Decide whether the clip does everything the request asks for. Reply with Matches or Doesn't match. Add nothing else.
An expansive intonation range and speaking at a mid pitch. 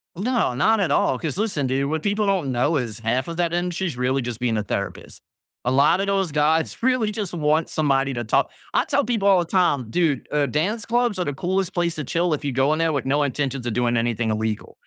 Matches